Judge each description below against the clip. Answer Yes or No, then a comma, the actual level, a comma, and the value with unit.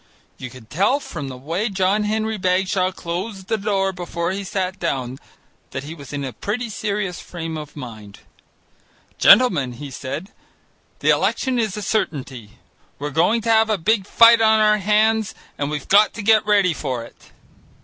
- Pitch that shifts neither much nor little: No, wide, 6.4 semitones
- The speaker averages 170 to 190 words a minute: Yes, average, 175 wpm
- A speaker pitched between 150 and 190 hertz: Yes, medium, 185 Hz